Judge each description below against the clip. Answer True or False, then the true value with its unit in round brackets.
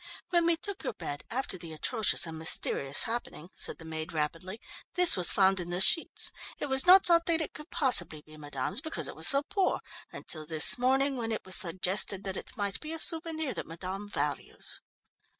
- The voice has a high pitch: True (205 Hz)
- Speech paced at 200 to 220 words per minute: True (205 wpm)